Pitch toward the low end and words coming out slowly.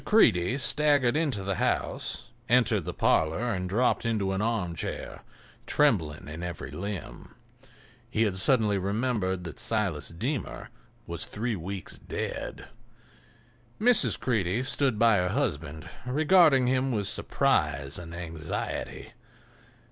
Yes: low, 105 Hz; slow, 120 wpm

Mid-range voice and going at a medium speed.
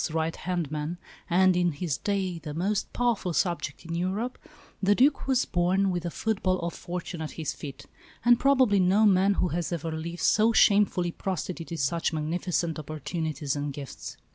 Yes: medium, 175 Hz; average, 175 wpm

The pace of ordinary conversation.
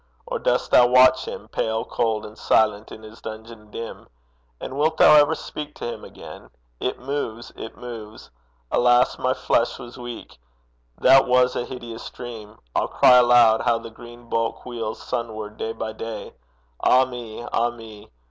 Yes: average, 165 wpm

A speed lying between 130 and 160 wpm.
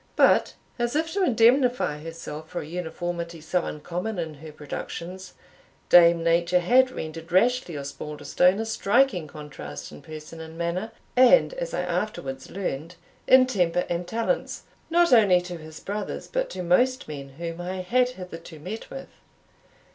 Yes: average, 155 wpm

